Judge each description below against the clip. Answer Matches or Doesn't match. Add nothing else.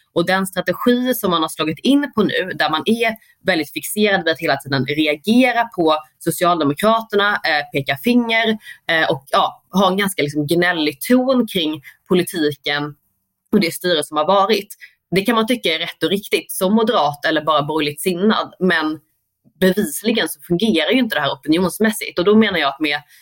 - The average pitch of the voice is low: Doesn't match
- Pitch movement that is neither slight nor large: Doesn't match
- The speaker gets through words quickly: Doesn't match